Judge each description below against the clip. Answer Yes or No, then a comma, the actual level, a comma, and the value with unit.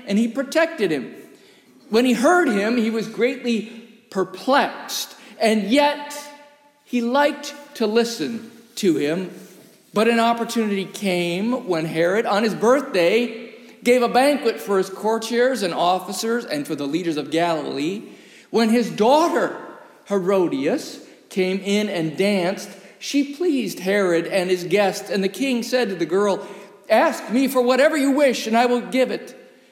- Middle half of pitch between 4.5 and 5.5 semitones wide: Yes, average, 5.0 semitones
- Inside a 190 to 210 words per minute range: No, average, 150 wpm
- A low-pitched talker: No, high, 230 Hz